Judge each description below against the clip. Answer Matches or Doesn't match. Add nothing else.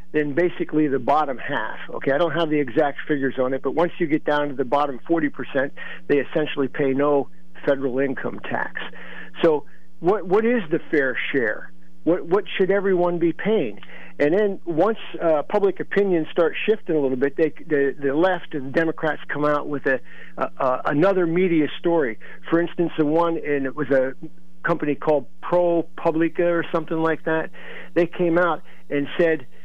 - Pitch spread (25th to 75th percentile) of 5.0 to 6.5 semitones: Doesn't match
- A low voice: Doesn't match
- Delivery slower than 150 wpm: Doesn't match